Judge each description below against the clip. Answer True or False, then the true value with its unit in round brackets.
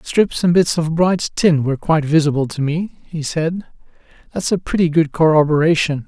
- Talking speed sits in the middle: True (180 wpm)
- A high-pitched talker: False (160 Hz)